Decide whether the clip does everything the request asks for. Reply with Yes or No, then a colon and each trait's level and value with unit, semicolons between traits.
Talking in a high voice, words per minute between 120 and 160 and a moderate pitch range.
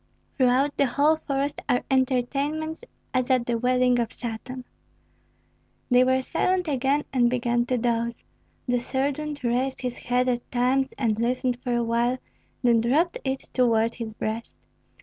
No: very high, 250 Hz; average, 155 wpm; narrow, 2.1 semitones